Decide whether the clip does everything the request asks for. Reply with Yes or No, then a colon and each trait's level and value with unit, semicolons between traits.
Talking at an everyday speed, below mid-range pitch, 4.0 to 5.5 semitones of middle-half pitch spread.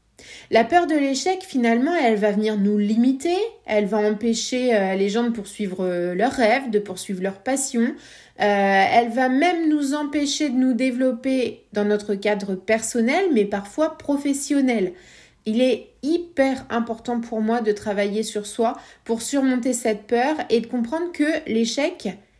No: average, 155 wpm; high, 235 Hz; average, 4.6 semitones